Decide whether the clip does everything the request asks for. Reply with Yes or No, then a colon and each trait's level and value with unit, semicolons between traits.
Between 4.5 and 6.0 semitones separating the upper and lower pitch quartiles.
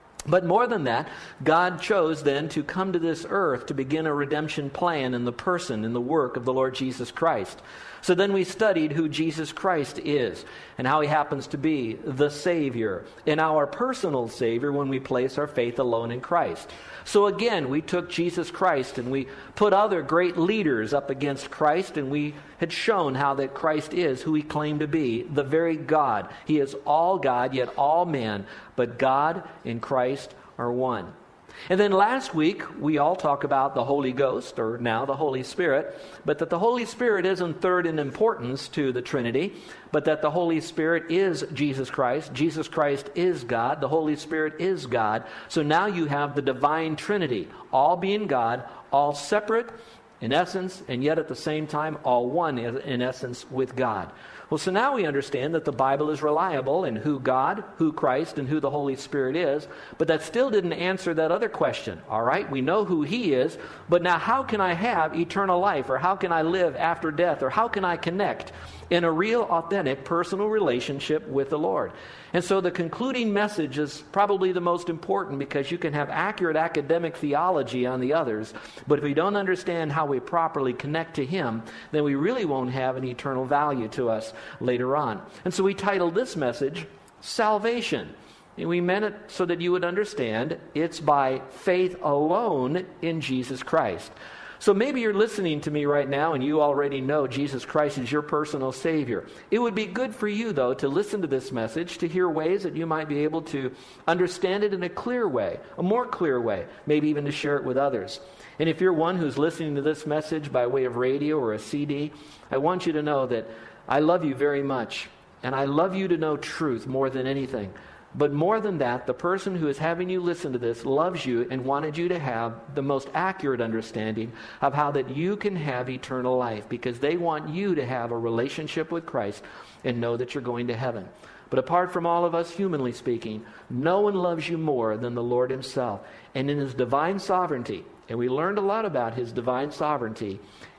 Yes: average, 4.9 semitones